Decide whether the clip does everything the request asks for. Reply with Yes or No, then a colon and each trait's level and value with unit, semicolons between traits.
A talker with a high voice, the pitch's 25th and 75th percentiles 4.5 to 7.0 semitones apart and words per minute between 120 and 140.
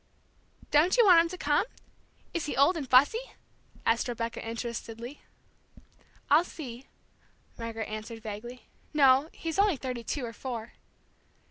Yes: very high, 255 Hz; average, 5.1 semitones; slow, 135 wpm